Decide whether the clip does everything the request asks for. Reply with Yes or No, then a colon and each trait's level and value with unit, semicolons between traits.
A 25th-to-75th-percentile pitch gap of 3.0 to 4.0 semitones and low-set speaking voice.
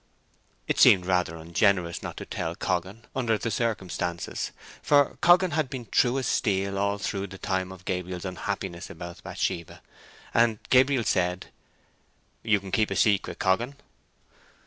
No: average, 4.4 semitones; low, 100 Hz